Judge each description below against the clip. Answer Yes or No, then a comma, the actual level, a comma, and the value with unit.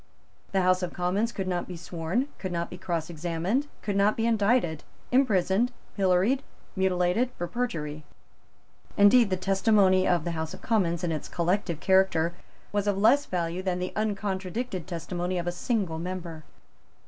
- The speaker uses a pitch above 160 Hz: Yes, medium, 185 Hz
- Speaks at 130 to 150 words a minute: No, average, 160 wpm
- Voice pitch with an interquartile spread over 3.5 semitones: No, average, 3.0 semitones